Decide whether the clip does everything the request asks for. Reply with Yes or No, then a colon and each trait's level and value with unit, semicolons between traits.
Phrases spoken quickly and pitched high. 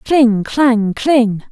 No: slow, 120 wpm; high, 240 Hz